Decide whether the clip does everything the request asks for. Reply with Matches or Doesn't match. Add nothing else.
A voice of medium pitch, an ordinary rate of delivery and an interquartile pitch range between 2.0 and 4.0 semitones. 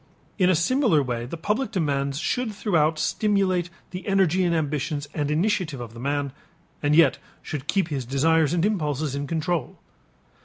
Doesn't match